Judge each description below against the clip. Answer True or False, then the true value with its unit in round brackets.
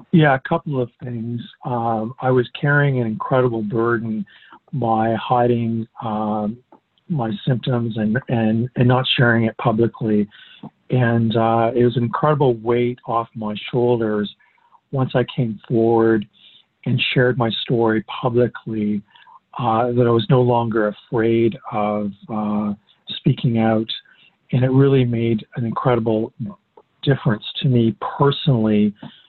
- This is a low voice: True (115 Hz)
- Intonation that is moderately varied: False (2.3 semitones)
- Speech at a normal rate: False (130 wpm)